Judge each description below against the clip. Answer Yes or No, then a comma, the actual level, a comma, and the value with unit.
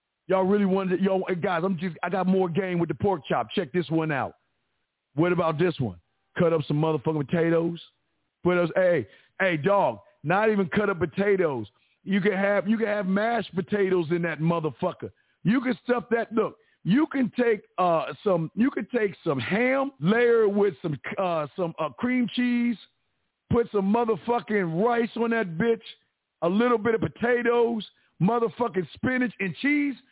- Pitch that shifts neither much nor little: Yes, average, 5.0 semitones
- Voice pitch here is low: No, high, 195 Hz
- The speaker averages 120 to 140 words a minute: No, average, 175 wpm